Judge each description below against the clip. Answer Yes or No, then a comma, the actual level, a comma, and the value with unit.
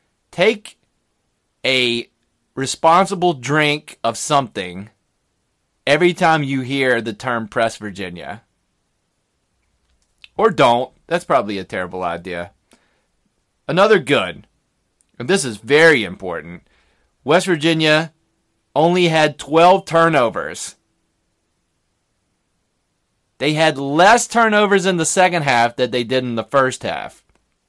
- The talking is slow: Yes, slow, 105 wpm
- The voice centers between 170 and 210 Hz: No, low, 130 Hz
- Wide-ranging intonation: Yes, wide, 7.8 semitones